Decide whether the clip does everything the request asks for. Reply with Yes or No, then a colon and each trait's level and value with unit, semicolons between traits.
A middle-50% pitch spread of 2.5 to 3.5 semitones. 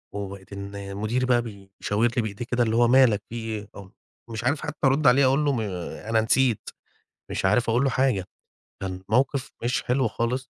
No: average, 4.0 semitones